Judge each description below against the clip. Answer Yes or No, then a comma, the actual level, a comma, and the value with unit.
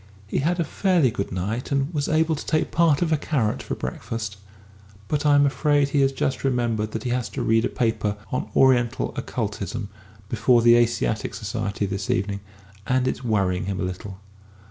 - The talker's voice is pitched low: Yes, low, 120 Hz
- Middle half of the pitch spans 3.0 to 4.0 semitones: No, average, 5.3 semitones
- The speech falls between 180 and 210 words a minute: Yes, average, 190 wpm